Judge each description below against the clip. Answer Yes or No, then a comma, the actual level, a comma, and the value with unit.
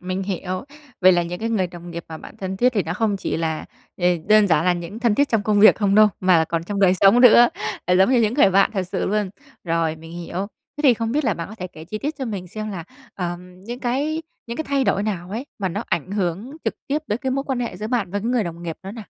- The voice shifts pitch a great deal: No, average, 4.4 semitones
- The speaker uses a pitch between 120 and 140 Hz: No, high, 200 Hz